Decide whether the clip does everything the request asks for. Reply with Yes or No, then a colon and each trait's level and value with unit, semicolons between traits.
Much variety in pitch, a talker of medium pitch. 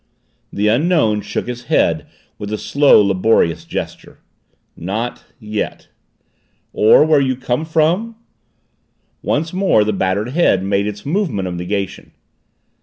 No: wide, 7.1 semitones; low, 110 Hz